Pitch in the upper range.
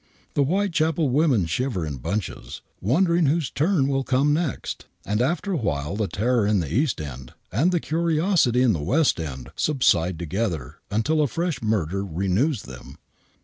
No: low, 125 Hz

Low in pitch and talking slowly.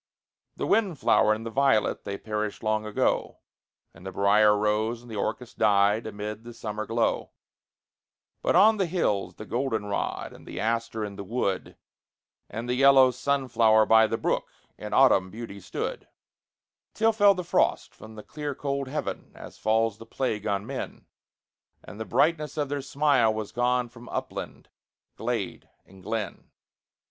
No: low, 115 Hz; average, 165 wpm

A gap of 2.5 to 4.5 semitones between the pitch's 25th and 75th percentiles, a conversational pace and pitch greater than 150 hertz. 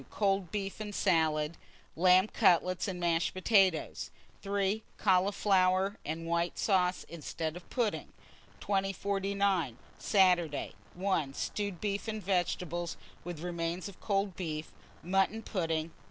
No: average, 2.8 semitones; slow, 115 wpm; medium, 185 Hz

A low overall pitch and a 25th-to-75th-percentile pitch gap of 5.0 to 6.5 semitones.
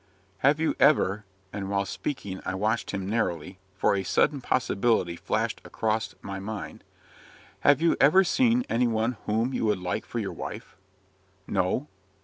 Yes: low, 110 Hz; wide, 5.5 semitones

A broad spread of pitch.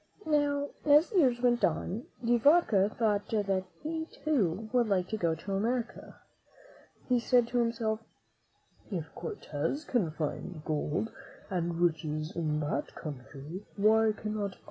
Yes: wide, 6.3 semitones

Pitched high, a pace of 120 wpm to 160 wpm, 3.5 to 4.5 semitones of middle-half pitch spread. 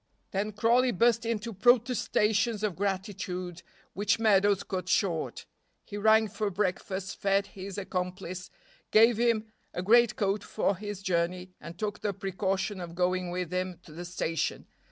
No: high, 195 Hz; average, 150 wpm; average, 2.8 semitones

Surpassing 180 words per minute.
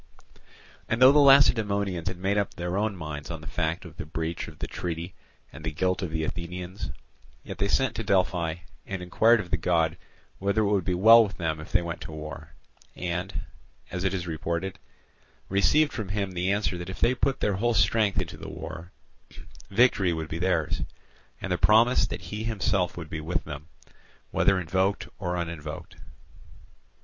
Yes: average, 190 wpm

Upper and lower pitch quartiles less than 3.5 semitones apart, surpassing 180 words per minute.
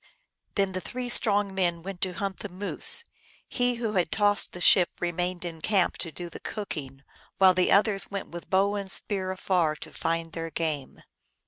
Yes: average, 2.9 semitones; average, 190 wpm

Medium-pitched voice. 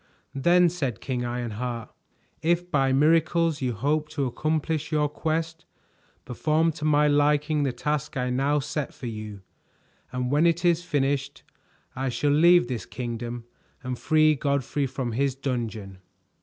Yes: medium, 145 Hz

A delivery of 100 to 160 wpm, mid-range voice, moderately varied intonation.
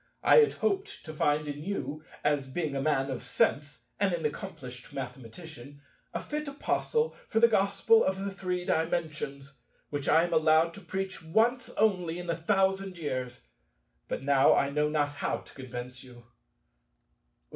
No: average, 155 wpm; medium, 155 Hz; wide, 5.7 semitones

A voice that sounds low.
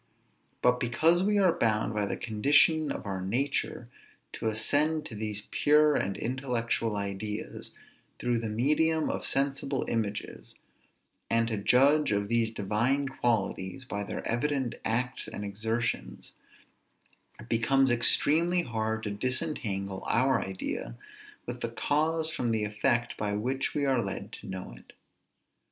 Yes: low, 115 Hz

